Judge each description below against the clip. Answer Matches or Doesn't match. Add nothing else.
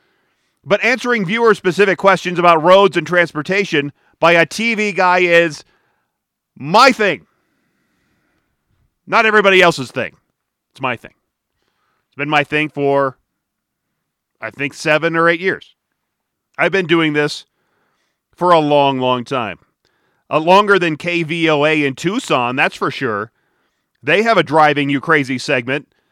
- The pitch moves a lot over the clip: Doesn't match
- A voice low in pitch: Doesn't match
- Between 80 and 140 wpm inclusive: Matches